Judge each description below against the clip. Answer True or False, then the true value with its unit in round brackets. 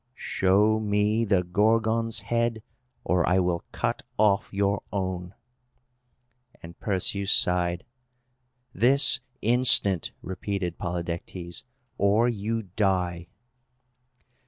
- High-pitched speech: False (100 Hz)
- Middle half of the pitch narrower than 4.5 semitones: True (3.4 semitones)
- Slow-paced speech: True (90 wpm)